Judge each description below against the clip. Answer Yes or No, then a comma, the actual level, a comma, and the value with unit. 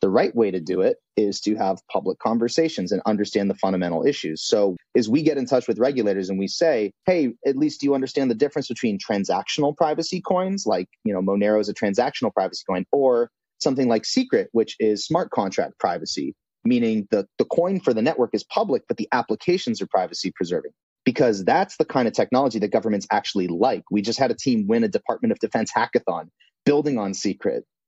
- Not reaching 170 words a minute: No, fast, 205 wpm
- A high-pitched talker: No, low, 130 Hz